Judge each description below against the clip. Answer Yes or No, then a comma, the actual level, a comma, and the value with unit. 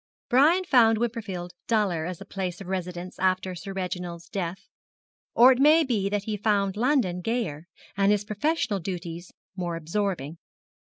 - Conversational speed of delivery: Yes, average, 155 wpm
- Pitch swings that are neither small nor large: Yes, average, 4.0 semitones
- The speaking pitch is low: No, high, 195 Hz